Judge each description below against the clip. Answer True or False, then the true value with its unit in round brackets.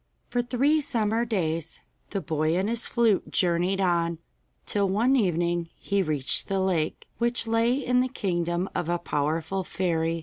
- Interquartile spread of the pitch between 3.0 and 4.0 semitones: False (5.3 semitones)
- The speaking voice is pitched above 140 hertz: True (190 Hz)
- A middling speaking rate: True (160 wpm)